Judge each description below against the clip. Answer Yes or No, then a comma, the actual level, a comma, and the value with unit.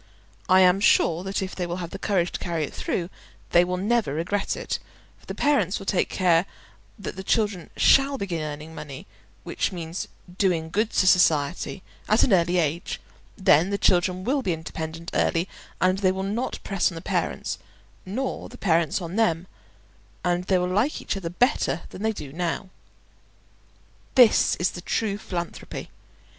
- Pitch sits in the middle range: Yes, medium, 180 Hz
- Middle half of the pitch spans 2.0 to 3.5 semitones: Yes, average, 2.8 semitones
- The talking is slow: No, average, 175 wpm